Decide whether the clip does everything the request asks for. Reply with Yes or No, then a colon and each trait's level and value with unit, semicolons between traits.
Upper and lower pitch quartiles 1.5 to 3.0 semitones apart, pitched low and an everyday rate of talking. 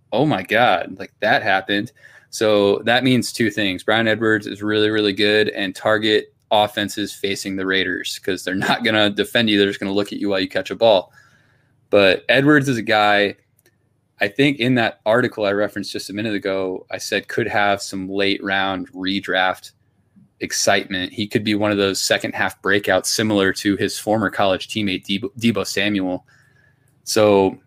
Yes: narrow, 2.5 semitones; low, 105 Hz; average, 185 wpm